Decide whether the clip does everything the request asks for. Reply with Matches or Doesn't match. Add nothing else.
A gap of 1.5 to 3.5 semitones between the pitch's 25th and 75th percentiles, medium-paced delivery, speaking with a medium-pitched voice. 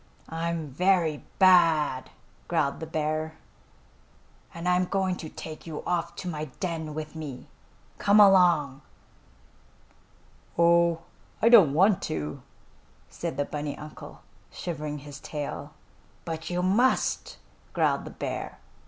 Doesn't match